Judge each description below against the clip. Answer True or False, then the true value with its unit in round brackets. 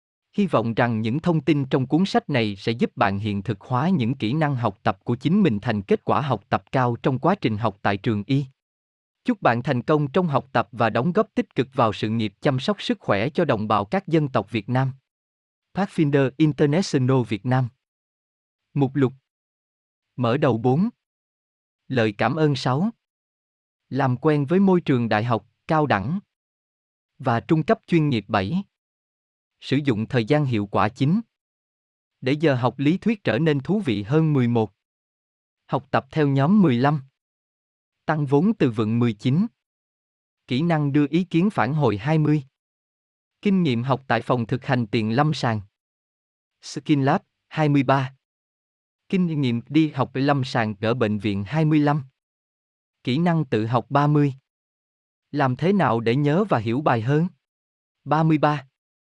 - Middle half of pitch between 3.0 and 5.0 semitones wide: False (5.4 semitones)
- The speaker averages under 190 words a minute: True (170 wpm)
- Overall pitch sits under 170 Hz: True (135 Hz)